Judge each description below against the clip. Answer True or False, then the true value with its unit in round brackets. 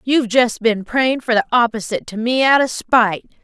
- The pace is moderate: False (210 wpm)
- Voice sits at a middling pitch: False (235 Hz)